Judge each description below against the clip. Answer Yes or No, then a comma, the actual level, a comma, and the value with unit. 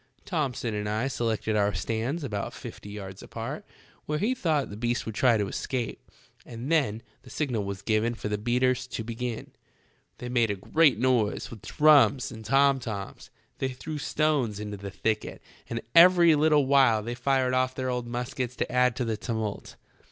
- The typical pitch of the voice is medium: No, low, 120 Hz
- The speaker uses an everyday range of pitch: Yes, average, 3.8 semitones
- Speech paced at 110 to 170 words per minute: No, average, 180 wpm